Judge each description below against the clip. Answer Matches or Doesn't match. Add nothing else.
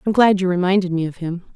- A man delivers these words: Doesn't match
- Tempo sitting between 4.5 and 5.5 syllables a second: Doesn't match